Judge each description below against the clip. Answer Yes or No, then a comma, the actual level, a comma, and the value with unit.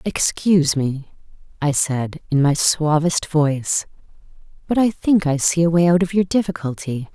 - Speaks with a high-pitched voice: No, medium, 160 Hz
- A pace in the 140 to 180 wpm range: Yes, average, 160 wpm